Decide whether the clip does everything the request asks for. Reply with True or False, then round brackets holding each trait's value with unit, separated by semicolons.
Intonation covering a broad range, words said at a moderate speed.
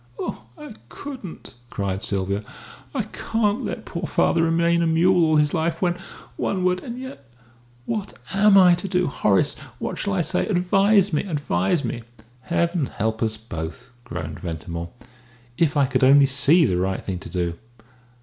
True (9.0 semitones; 170 wpm)